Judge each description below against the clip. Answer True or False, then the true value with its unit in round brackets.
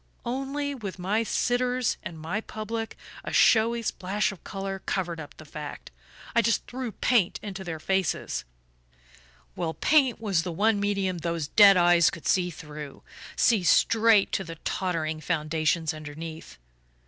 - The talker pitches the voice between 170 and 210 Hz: True (190 Hz)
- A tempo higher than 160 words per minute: False (150 wpm)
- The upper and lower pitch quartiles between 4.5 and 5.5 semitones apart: True (5.2 semitones)